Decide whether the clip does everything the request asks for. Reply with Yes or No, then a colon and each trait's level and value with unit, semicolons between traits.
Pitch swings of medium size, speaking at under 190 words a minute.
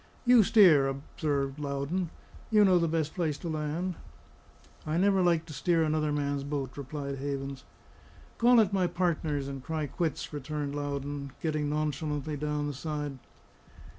Yes: average, 3.0 semitones; average, 150 wpm